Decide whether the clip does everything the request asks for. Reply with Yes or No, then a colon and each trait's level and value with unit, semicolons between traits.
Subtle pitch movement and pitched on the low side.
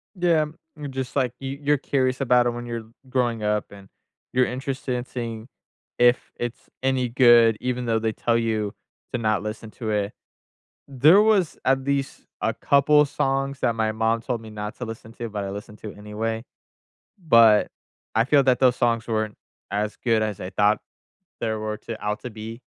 No: average, 3.2 semitones; low, 115 Hz